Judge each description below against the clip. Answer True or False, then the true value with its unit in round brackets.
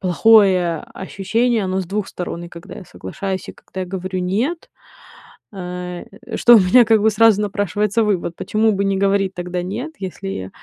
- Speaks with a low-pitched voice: False (195 Hz)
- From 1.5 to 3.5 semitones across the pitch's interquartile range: True (2.8 semitones)